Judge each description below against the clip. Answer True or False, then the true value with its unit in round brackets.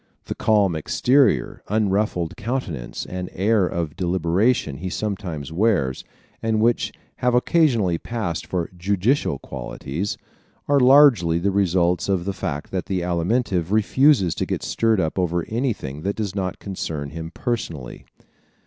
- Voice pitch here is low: True (95 Hz)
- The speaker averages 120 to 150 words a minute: True (140 wpm)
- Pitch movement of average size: True (4.8 semitones)